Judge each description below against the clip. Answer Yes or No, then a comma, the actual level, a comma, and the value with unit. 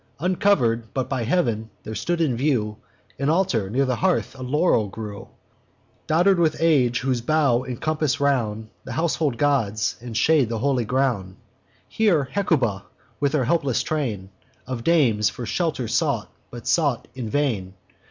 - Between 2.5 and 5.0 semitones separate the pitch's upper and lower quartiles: No, wide, 5.4 semitones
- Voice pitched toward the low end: Yes, low, 130 Hz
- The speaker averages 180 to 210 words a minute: No, average, 155 wpm